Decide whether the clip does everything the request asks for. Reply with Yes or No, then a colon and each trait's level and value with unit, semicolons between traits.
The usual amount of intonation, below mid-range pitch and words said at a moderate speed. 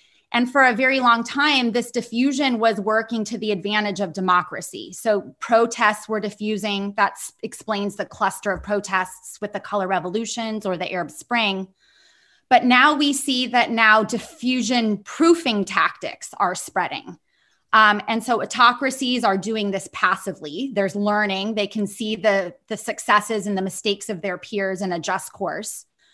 No: average, 3.3 semitones; high, 215 Hz; average, 160 wpm